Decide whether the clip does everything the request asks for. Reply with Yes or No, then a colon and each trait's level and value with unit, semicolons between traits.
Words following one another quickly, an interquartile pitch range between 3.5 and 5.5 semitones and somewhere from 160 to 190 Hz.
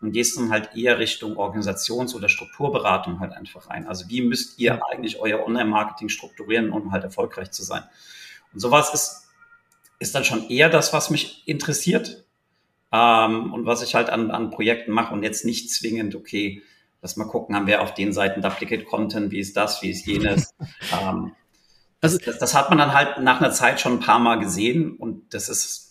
No: fast, 195 wpm; average, 4.7 semitones; low, 115 Hz